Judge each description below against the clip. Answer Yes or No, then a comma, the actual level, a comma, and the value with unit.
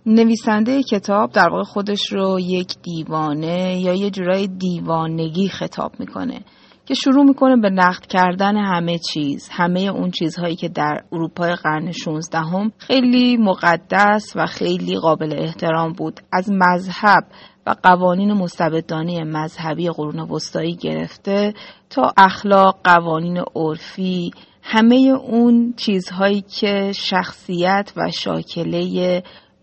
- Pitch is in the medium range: Yes, medium, 180 Hz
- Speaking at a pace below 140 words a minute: Yes, average, 115 wpm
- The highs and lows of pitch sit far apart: No, average, 3.4 semitones